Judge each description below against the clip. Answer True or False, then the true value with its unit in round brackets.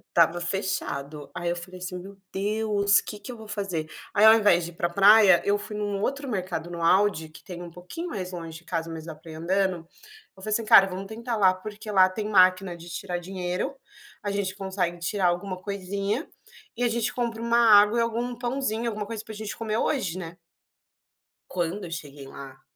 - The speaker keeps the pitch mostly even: False (3.6 semitones)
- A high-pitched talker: True (195 Hz)